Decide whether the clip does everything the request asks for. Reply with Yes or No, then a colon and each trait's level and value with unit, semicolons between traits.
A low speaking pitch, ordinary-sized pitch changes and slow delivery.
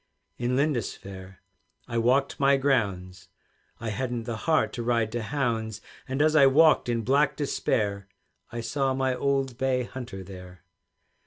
No: low, 120 Hz; average, 3.8 semitones; average, 150 wpm